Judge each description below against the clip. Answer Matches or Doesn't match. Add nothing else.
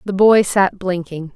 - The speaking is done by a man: Doesn't match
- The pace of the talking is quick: Doesn't match